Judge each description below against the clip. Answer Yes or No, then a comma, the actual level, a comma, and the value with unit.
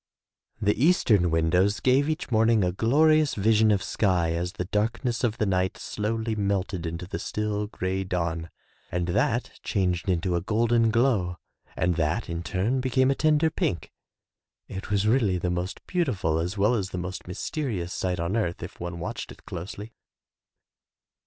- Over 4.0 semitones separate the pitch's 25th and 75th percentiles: Yes, average, 4.4 semitones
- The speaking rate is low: No, average, 170 wpm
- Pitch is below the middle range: Yes, low, 100 Hz